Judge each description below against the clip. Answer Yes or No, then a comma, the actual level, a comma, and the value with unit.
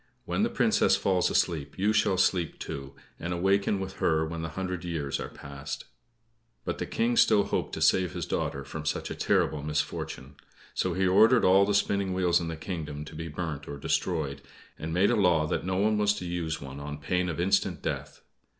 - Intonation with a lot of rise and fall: No, average, 3.9 semitones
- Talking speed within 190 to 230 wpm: Yes, fast, 205 wpm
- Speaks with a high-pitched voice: No, very low, 85 Hz